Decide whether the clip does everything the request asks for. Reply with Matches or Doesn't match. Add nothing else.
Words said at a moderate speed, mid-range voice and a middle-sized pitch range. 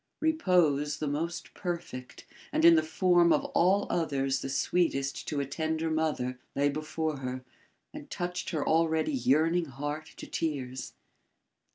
Matches